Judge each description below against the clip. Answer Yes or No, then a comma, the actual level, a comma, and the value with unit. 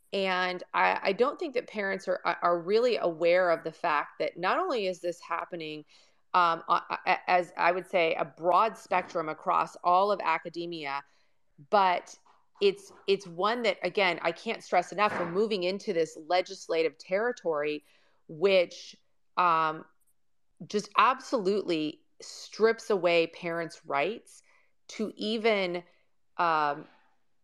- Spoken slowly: Yes, slow, 130 wpm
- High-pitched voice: No, medium, 180 Hz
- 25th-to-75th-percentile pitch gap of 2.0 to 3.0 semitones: No, average, 3.7 semitones